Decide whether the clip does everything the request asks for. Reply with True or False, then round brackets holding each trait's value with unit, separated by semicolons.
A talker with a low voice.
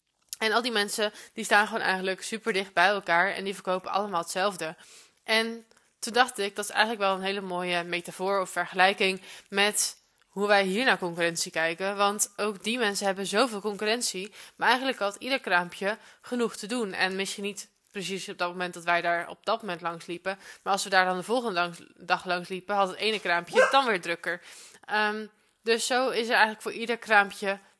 False (200 Hz)